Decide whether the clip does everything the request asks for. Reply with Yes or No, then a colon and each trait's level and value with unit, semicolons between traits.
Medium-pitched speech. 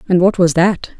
Yes: medium, 180 Hz